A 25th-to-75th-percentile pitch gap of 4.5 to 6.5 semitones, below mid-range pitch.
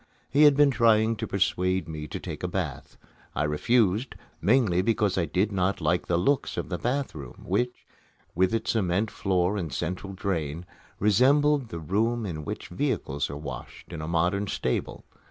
Yes: average, 4.9 semitones; very low, 95 Hz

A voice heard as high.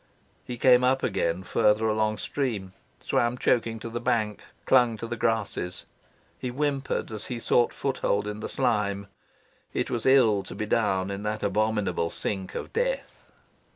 No: low, 110 Hz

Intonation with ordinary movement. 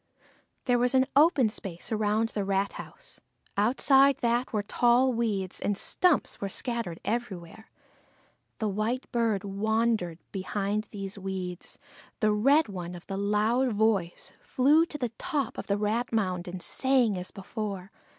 Yes: average, 3.8 semitones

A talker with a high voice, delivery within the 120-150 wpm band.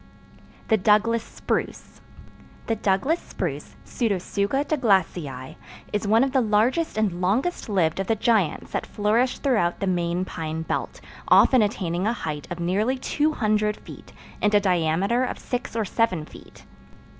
Yes: high, 210 Hz; average, 145 wpm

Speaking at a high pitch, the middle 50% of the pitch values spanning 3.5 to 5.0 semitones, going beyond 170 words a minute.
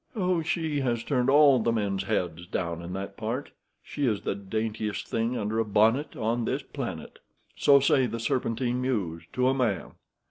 No: low, 115 Hz; average, 4.4 semitones; average, 180 wpm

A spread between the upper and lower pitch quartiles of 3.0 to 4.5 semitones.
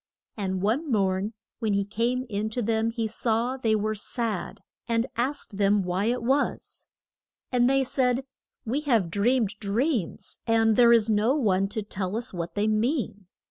Yes: average, 3.3 semitones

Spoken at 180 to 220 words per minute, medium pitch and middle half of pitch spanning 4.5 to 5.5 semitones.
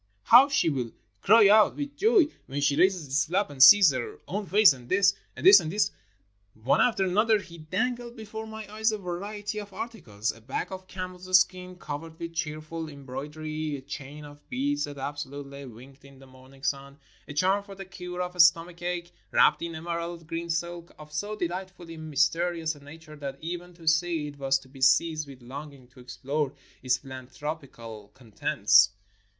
Yes: average, 190 wpm; medium, 165 Hz; average, 5.1 semitones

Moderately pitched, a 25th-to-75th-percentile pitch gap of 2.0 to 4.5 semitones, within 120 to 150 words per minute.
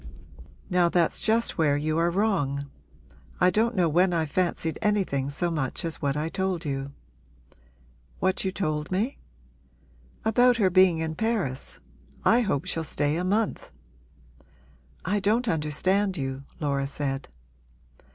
No: medium, 170 Hz; average, 5.0 semitones; average, 140 wpm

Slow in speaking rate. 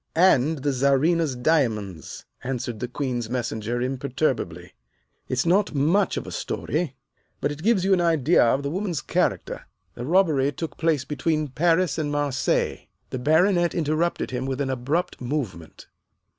No: average, 150 wpm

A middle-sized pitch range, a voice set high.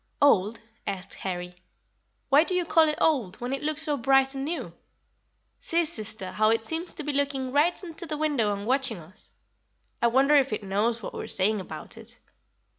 No: wide, 6.2 semitones; very high, 265 Hz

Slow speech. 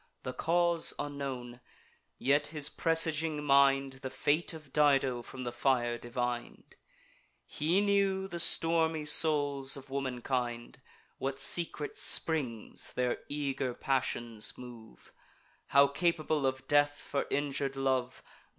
Yes: slow, 115 wpm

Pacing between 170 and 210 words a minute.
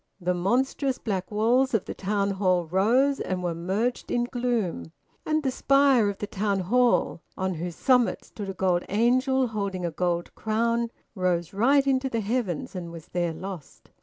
Yes: average, 175 wpm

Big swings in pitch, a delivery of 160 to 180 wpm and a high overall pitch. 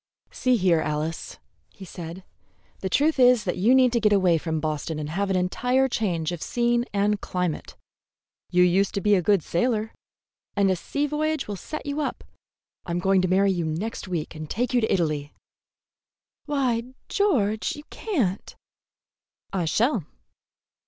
Yes: wide, 5.8 semitones; average, 165 wpm; high, 195 Hz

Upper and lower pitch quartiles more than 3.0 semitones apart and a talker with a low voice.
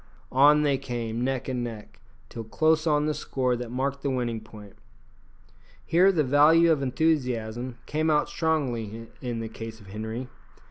Yes: average, 4.6 semitones; low, 130 Hz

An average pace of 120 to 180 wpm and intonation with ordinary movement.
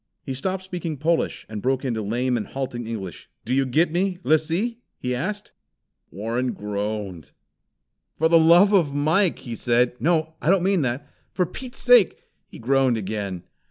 No: average, 170 wpm; wide, 6.8 semitones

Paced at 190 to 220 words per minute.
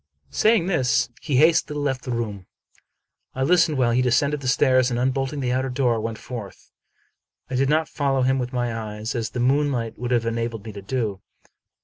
Yes: average, 200 wpm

